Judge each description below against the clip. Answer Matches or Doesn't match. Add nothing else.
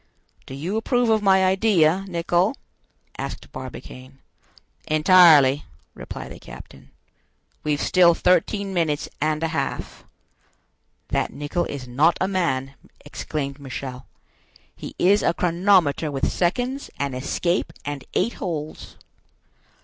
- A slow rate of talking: Matches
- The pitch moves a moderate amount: Matches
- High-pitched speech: Doesn't match